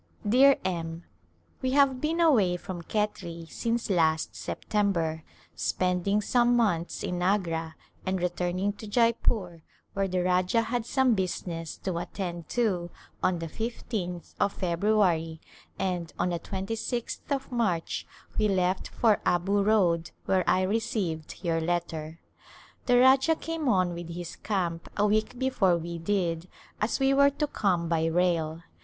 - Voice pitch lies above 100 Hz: Yes, medium, 185 Hz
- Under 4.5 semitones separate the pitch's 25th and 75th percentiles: No, average, 4.8 semitones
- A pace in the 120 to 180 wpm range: Yes, average, 150 wpm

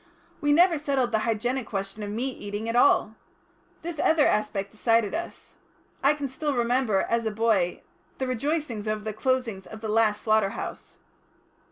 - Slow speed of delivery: No, average, 170 wpm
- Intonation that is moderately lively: Yes, average, 3.9 semitones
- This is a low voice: No, high, 230 Hz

